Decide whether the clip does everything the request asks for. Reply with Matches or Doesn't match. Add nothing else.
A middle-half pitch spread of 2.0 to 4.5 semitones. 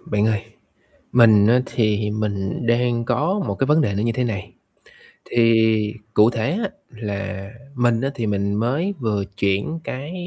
Matches